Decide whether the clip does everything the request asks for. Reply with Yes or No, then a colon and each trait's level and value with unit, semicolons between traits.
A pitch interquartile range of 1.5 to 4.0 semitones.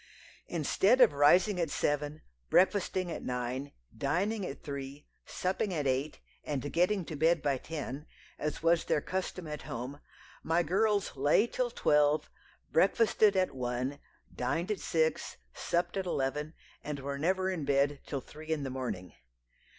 No: average, 4.6 semitones